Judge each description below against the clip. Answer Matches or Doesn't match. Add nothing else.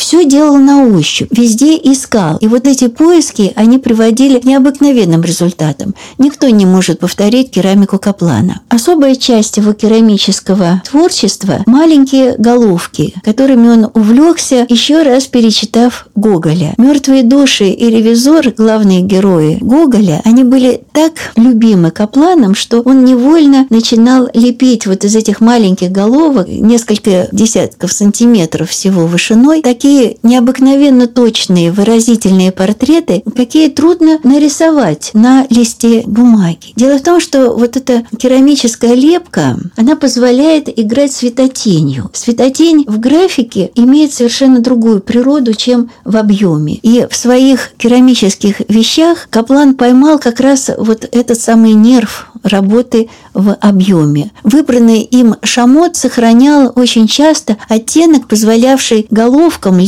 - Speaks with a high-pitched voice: Matches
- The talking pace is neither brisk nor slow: Matches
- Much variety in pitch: Doesn't match